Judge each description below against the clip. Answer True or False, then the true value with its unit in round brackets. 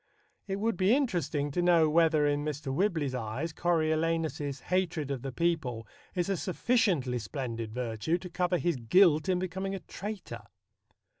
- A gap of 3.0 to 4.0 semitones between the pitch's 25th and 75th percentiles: False (4.7 semitones)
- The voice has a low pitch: False (165 Hz)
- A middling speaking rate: True (155 wpm)